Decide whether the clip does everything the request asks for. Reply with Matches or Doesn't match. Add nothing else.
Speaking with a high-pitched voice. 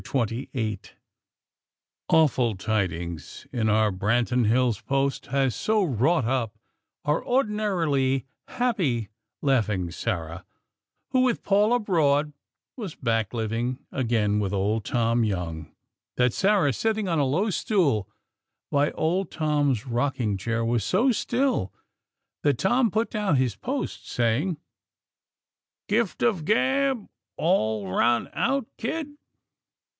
Doesn't match